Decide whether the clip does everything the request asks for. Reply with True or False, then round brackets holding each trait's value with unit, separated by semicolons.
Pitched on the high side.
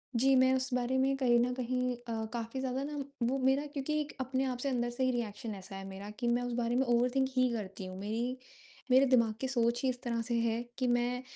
True (245 Hz)